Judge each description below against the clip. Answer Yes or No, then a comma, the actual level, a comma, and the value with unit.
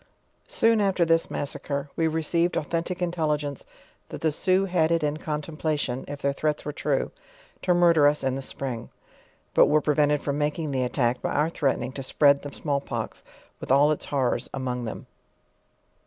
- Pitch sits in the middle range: Yes, medium, 150 Hz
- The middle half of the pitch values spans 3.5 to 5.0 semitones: No, average, 2.9 semitones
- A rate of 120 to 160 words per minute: No, average, 180 wpm